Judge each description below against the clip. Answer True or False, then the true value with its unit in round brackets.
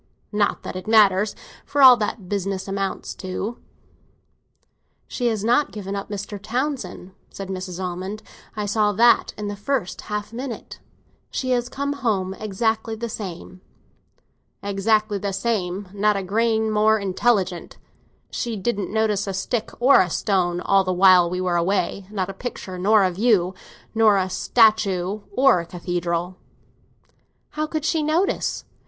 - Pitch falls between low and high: False (205 Hz)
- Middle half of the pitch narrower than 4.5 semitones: True (3.2 semitones)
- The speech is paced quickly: False (150 wpm)